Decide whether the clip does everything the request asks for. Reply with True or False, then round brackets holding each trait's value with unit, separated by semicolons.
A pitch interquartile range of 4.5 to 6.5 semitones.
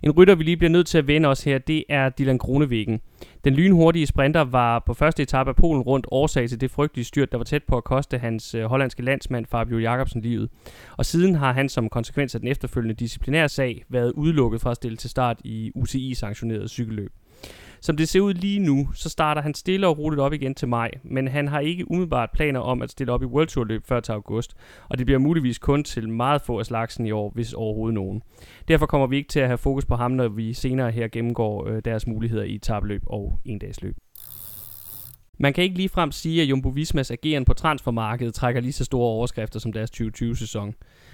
False (4.0 semitones)